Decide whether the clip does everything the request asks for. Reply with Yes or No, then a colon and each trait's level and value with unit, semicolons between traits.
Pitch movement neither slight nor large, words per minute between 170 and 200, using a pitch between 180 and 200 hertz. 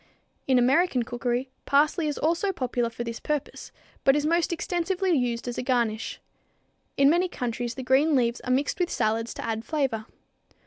No: average, 4.9 semitones; average, 175 wpm; very high, 260 Hz